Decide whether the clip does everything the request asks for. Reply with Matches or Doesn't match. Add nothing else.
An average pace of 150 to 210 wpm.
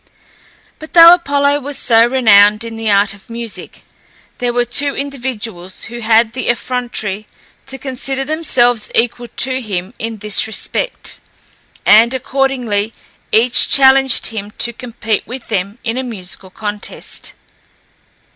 Doesn't match